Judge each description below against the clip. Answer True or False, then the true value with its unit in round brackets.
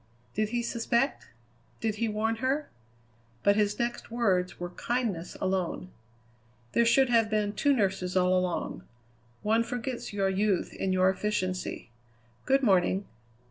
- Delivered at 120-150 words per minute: True (140 wpm)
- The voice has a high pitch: True (210 Hz)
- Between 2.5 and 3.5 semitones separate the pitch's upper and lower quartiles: False (4.0 semitones)